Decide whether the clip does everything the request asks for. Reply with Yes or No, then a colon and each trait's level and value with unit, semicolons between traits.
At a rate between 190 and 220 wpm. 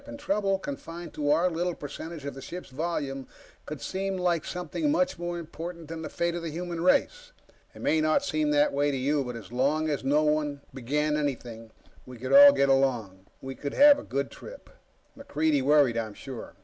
Yes: average, 200 wpm